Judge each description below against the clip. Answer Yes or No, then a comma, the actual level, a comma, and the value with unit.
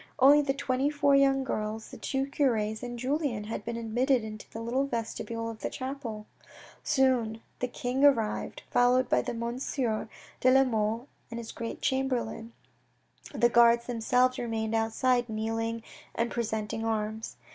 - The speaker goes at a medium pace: Yes, average, 150 wpm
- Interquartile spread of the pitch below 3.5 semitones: Yes, average, 2.8 semitones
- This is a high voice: Yes, high, 235 Hz